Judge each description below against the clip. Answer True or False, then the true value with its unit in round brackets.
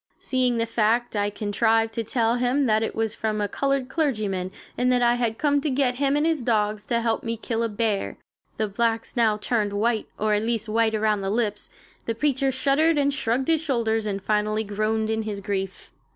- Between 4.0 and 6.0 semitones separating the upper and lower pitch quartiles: False (2.8 semitones)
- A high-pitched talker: True (225 Hz)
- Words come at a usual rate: False (210 wpm)